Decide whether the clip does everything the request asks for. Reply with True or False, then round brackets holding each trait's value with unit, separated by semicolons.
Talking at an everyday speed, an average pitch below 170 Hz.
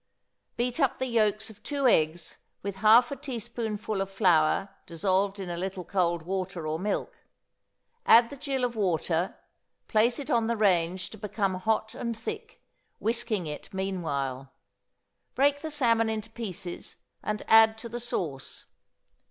False (150 wpm; 210 Hz)